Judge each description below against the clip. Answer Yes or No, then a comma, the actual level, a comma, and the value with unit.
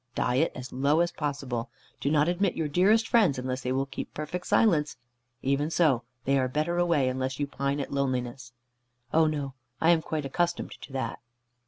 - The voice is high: No, medium, 145 Hz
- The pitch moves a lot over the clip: No, average, 3.8 semitones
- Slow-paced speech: No, average, 185 wpm